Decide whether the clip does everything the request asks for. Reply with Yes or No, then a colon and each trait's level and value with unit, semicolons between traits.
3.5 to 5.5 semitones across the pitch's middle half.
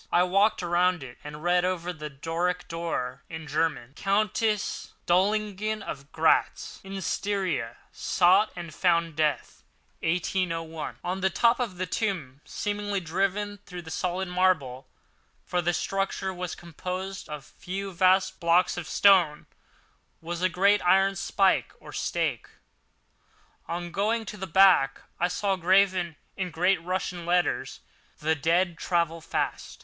No: average, 2.8 semitones